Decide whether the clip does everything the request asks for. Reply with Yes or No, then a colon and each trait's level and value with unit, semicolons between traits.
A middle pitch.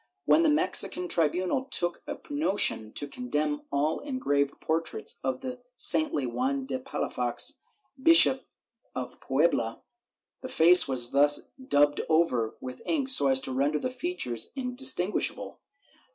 Yes: medium, 165 Hz